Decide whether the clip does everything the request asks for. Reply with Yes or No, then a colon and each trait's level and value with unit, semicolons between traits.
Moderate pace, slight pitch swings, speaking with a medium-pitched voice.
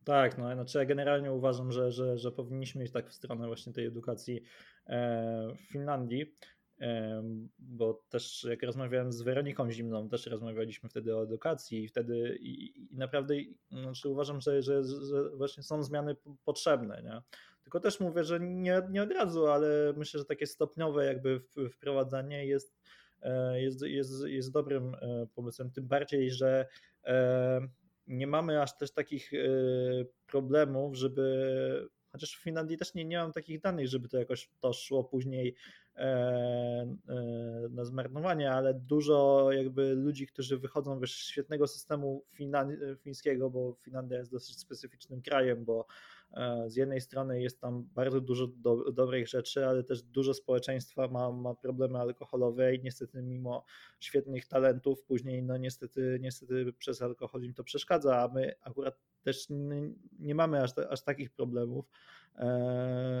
No: average, 145 wpm; narrow, 2.2 semitones; low, 130 Hz